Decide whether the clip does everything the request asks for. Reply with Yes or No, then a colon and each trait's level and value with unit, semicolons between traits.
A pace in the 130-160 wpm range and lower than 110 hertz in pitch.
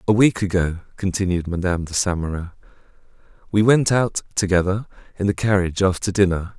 Yes: average, 155 wpm; very low, 95 Hz